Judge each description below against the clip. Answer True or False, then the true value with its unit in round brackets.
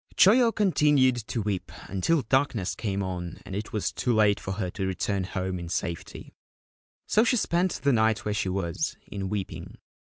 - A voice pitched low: True (105 Hz)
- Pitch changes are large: True (6.1 semitones)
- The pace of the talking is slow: False (175 wpm)